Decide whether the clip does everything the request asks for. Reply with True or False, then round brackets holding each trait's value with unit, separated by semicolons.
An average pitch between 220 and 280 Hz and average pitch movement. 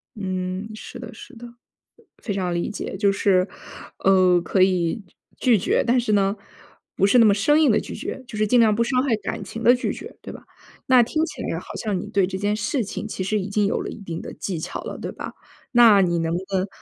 False (205 Hz; 3.7 semitones)